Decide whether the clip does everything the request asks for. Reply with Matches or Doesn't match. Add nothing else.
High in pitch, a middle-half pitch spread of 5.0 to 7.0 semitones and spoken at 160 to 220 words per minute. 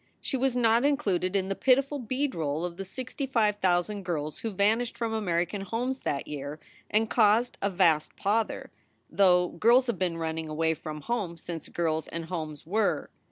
Matches